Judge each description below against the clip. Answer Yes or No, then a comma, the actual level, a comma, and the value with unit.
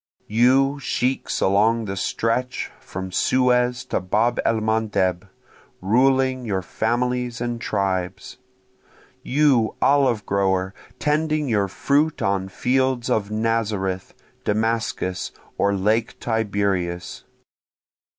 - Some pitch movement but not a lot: Yes, average, 4.2 semitones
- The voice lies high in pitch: No, low, 110 Hz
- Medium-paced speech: No, slow, 100 wpm